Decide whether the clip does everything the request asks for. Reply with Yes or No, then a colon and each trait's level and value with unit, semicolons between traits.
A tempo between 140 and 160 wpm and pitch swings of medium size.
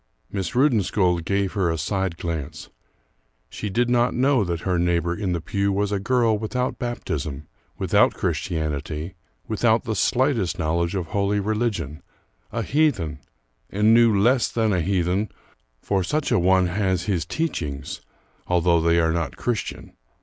Yes: average, 150 wpm; average, 4.6 semitones